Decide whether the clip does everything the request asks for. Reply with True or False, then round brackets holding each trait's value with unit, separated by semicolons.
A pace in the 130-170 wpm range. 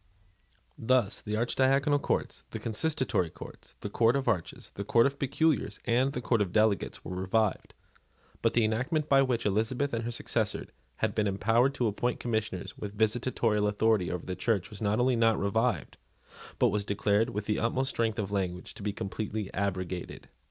False (180 wpm)